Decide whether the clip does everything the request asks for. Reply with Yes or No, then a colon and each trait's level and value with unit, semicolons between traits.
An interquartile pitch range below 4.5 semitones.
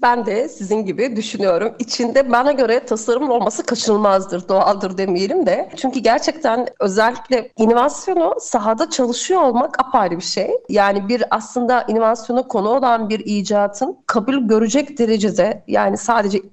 Yes: average, 3.5 semitones